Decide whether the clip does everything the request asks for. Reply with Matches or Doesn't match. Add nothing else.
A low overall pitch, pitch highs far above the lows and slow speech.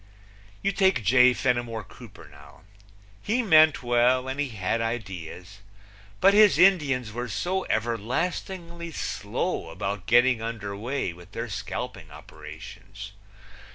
Matches